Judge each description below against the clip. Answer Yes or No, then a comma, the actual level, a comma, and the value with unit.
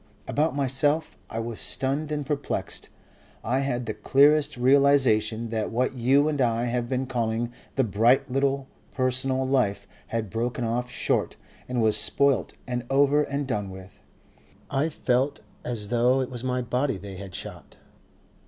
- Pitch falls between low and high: No, low, 125 Hz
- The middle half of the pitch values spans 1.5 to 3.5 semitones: Yes, average, 3.1 semitones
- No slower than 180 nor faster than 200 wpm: No, average, 155 wpm